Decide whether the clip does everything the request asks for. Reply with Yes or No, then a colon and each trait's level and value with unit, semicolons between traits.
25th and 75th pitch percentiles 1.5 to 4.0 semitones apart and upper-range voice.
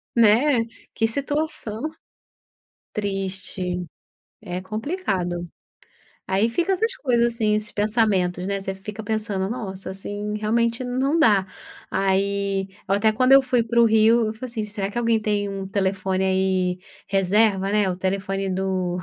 Yes: average, 3.1 semitones; high, 205 Hz